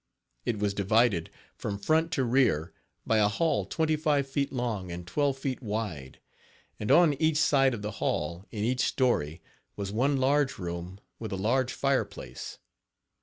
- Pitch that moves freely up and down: Yes, wide, 5.8 semitones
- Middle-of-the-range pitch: No, low, 115 Hz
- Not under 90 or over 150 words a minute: No, average, 170 wpm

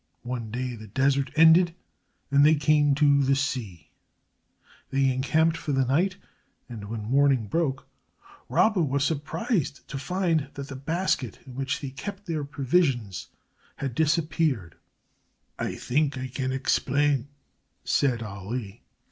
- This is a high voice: No, medium, 140 Hz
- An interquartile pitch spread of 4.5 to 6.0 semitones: No, average, 3.5 semitones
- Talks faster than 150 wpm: No, slow, 135 wpm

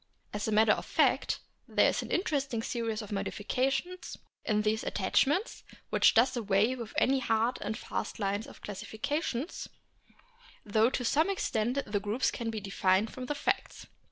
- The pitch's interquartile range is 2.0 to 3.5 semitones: No, average, 3.9 semitones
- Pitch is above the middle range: Yes, high, 225 Hz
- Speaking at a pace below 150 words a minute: No, average, 165 wpm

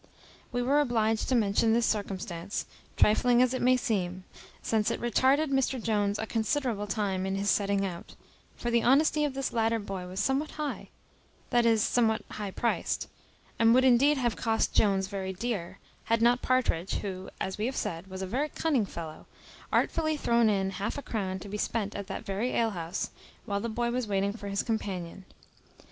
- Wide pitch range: No, average, 3.9 semitones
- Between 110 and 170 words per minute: No, average, 190 wpm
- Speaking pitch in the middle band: No, high, 220 Hz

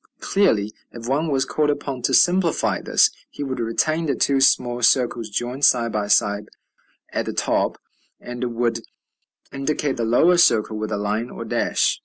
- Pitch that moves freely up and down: No, average, 3.9 semitones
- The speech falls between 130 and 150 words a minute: No, average, 170 wpm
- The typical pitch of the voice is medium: No, low, 125 Hz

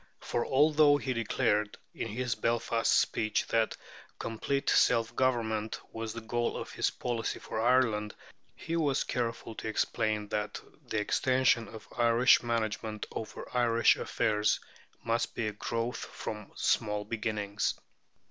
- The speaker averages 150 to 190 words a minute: No, slow, 135 wpm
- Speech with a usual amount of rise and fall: No, narrow, 2.0 semitones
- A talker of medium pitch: No, low, 115 Hz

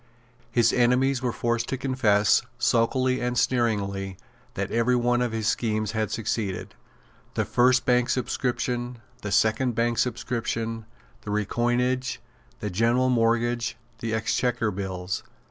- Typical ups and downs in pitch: No, narrow, 2.3 semitones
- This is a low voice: Yes, low, 120 Hz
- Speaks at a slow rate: Yes, slow, 130 wpm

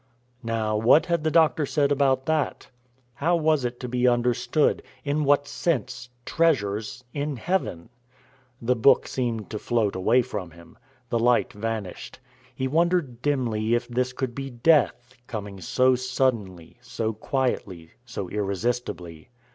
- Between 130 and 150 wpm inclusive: Yes, average, 140 wpm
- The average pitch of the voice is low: Yes, low, 125 Hz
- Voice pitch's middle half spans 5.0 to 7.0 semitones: No, average, 4.3 semitones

